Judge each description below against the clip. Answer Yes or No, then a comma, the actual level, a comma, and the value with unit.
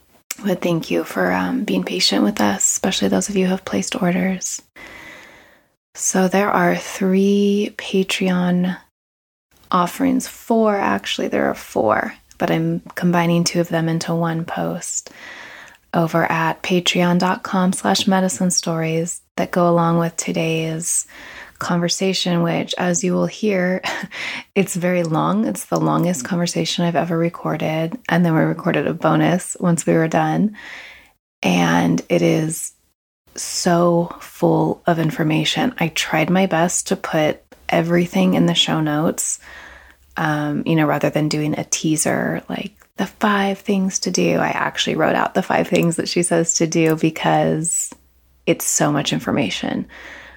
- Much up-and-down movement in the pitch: No, average, 2.7 semitones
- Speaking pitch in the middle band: Yes, medium, 170 Hz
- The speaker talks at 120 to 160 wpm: Yes, average, 145 wpm